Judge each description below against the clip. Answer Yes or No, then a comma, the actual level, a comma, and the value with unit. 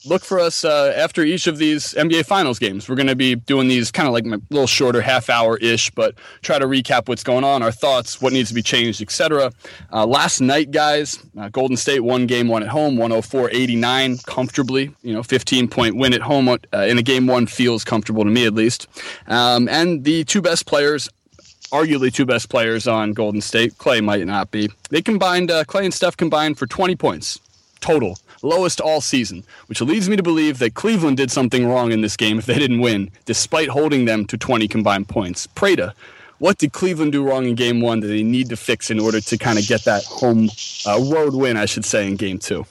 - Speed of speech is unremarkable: No, fast, 220 wpm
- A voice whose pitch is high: No, low, 125 Hz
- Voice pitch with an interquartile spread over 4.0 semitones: Yes, average, 4.7 semitones